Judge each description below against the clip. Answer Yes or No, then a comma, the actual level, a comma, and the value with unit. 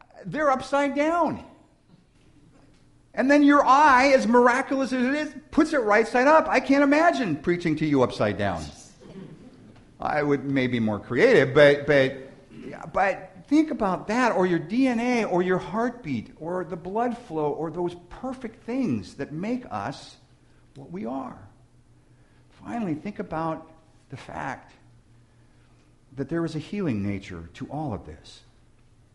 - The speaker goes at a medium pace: Yes, average, 145 wpm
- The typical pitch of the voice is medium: Yes, medium, 180 Hz